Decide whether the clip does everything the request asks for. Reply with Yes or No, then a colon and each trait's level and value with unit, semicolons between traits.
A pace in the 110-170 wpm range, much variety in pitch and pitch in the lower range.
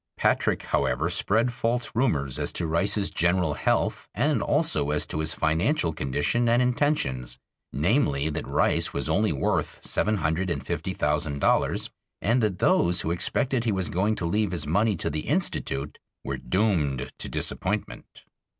Yes: average, 160 wpm; wide, 6.6 semitones; very low, 90 Hz